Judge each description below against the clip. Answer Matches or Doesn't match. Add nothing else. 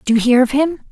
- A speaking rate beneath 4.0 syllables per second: Doesn't match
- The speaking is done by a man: Doesn't match